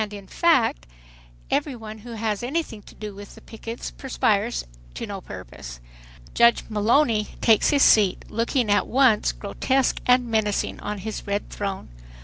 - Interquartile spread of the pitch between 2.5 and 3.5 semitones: Yes, average, 2.8 semitones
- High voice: Yes, high, 220 Hz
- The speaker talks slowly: No, average, 150 wpm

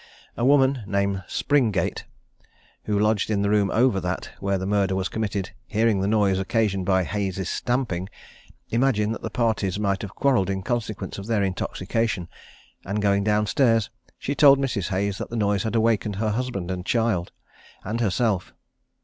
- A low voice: Yes, low, 105 Hz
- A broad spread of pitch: No, average, 2.9 semitones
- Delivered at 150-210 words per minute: Yes, average, 170 wpm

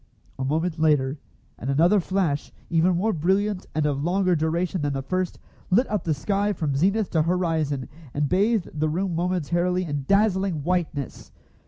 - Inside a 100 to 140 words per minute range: No, average, 165 wpm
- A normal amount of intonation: Yes, average, 3.9 semitones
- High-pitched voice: No, medium, 170 Hz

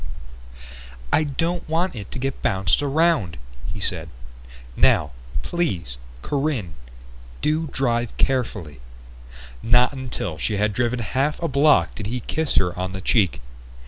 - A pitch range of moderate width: No, wide, 7.1 semitones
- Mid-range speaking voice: No, low, 125 Hz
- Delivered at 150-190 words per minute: No, slow, 135 wpm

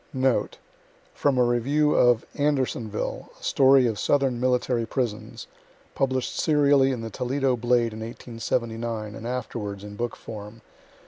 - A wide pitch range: No, average, 2.7 semitones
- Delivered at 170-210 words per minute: No, slow, 135 wpm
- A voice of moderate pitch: No, low, 120 Hz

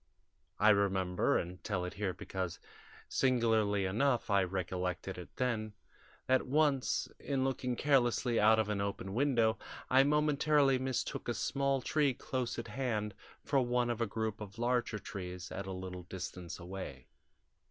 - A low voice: Yes, low, 110 Hz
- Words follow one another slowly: No, average, 150 wpm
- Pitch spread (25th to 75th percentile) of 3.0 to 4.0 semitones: No, average, 5.3 semitones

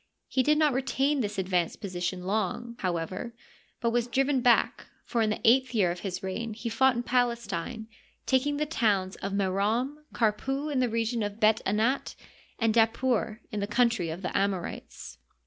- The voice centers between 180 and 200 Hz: No, high, 225 Hz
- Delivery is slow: No, average, 175 wpm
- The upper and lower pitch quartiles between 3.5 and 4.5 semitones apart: Yes, average, 4.1 semitones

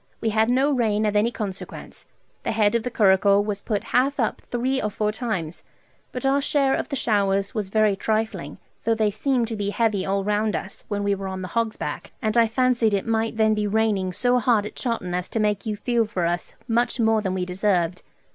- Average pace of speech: No, fast, 225 wpm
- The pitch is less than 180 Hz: No, high, 215 Hz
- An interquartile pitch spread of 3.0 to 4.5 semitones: No, narrow, 2.6 semitones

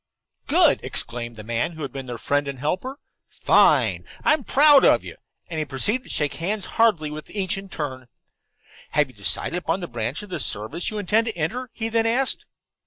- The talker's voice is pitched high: No, medium, 165 Hz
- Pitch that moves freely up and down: Yes, wide, 8.6 semitones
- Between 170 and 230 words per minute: Yes, average, 200 wpm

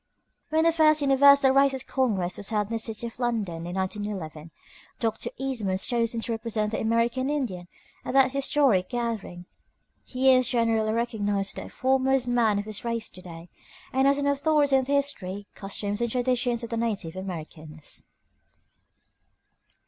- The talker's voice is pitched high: Yes, high, 230 Hz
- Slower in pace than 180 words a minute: Yes, average, 165 wpm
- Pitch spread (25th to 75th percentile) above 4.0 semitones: Yes, average, 4.7 semitones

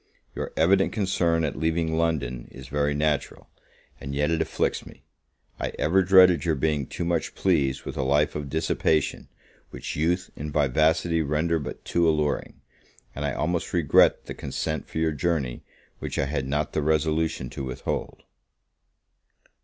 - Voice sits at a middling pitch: No, very low, 80 Hz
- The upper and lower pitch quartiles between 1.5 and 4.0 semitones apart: Yes, narrow, 2.5 semitones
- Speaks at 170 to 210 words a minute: No, average, 160 wpm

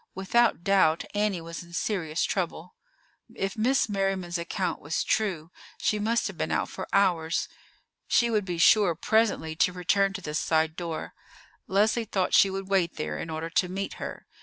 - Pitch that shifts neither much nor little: Yes, average, 3.4 semitones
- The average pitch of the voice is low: No, medium, 185 Hz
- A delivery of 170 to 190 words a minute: Yes, average, 175 wpm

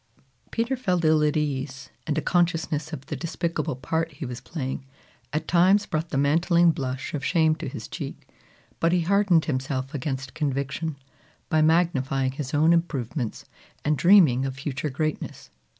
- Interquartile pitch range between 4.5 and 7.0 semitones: No, average, 3.6 semitones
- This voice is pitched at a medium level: Yes, medium, 155 Hz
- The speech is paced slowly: No, average, 160 wpm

